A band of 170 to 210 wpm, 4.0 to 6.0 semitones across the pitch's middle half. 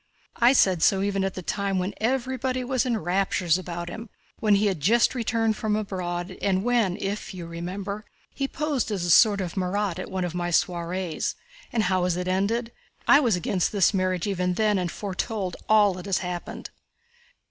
No: average, 190 wpm; average, 3.3 semitones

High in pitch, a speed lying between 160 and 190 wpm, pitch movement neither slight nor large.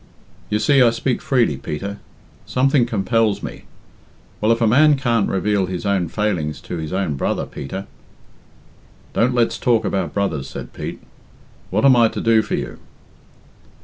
No: low, 105 Hz; average, 165 wpm; average, 3.9 semitones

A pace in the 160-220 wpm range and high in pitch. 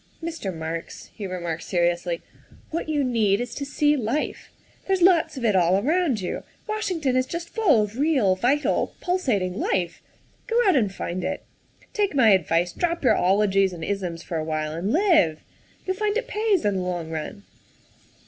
Yes: average, 185 wpm; high, 215 Hz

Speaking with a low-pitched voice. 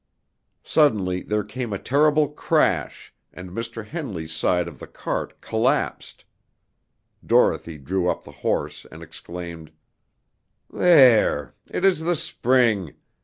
Yes: low, 110 Hz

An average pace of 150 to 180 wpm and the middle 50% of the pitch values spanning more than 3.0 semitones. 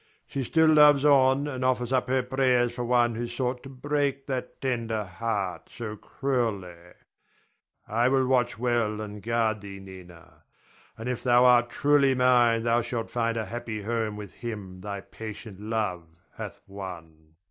Yes: average, 160 wpm; average, 3.4 semitones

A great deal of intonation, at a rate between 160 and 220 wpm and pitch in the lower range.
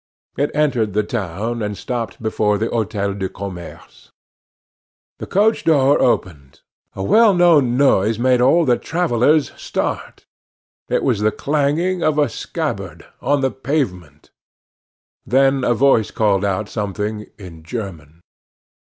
No: wide, 5.7 semitones; slow, 135 wpm; low, 115 Hz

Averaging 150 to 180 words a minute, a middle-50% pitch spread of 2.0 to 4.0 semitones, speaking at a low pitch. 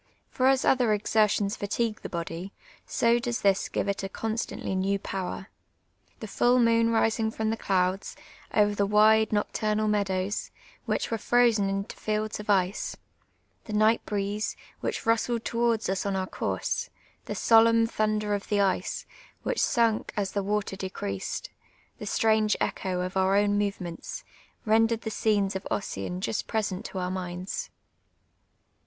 No: average, 155 wpm; narrow, 2.4 semitones; high, 210 Hz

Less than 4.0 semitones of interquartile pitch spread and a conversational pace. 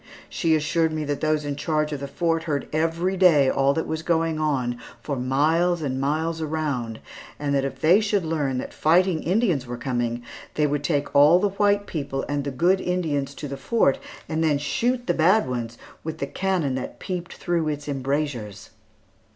Yes: average, 3.3 semitones; average, 190 wpm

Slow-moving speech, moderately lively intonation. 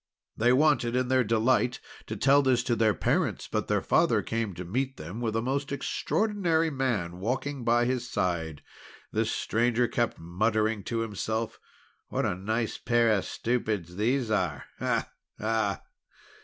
No: average, 155 wpm; average, 3.2 semitones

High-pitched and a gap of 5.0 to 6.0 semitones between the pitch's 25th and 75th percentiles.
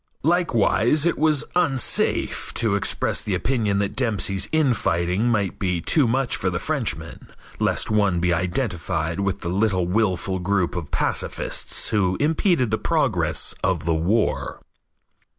No: low, 100 Hz; wide, 5.6 semitones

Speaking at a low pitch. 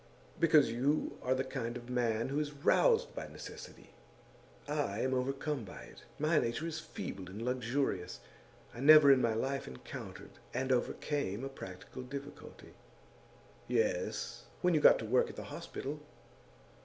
Yes: low, 130 Hz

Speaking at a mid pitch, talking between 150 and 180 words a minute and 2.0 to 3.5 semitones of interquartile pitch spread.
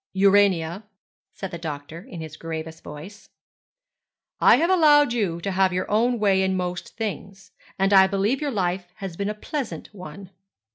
No: high, 195 Hz; average, 170 wpm; average, 3.1 semitones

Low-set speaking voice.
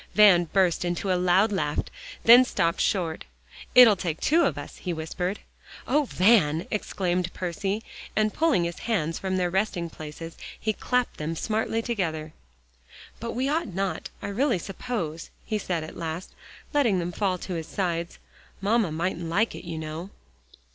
No: medium, 185 Hz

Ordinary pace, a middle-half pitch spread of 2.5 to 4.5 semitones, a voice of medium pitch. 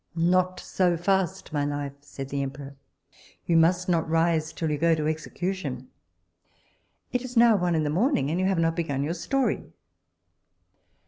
Yes: average, 170 wpm; average, 3.8 semitones; medium, 165 Hz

